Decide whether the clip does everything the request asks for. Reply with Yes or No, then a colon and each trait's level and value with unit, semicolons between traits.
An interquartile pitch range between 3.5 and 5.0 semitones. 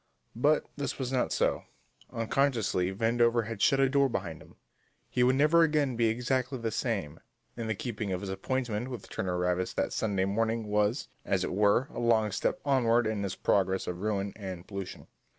Yes: average, 4.3 semitones